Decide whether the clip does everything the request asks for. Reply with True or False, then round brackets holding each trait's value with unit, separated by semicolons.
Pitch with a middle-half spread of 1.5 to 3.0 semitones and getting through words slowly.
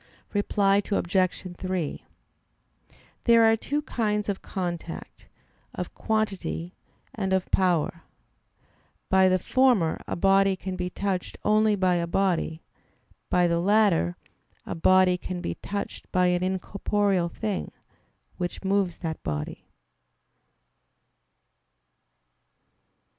True (2.4 semitones; 110 wpm)